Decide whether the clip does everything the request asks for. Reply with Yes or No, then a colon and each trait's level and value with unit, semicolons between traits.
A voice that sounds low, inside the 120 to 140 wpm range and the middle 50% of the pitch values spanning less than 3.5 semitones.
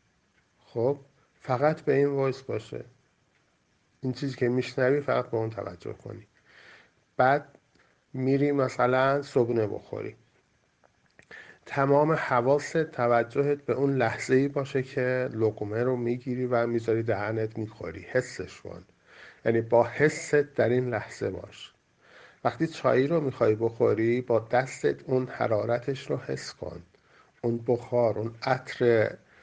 Yes: low, 125 Hz; average, 125 wpm; average, 2.8 semitones